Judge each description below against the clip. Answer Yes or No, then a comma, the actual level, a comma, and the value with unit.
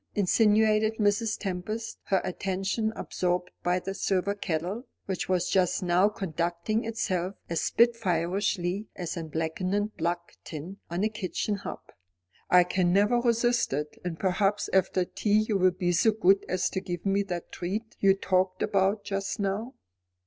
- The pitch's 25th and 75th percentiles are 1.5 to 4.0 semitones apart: Yes, average, 2.9 semitones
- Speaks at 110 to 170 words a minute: Yes, average, 155 wpm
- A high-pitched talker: Yes, high, 195 Hz